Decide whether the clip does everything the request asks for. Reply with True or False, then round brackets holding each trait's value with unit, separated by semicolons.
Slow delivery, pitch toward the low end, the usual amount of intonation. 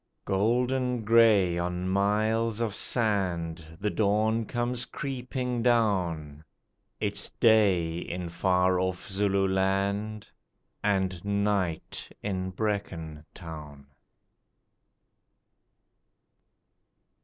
True (75 wpm; 100 Hz; 3.7 semitones)